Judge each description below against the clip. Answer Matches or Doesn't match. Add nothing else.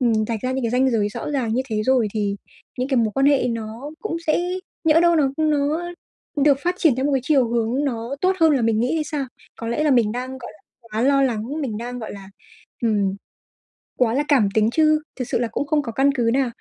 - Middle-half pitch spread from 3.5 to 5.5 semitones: Matches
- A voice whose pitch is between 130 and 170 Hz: Doesn't match